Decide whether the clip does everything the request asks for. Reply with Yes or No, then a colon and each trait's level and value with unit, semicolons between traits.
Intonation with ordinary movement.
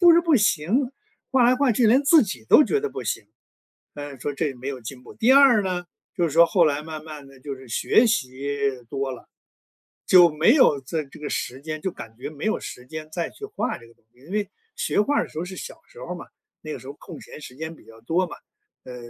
No: wide, 8.6 semitones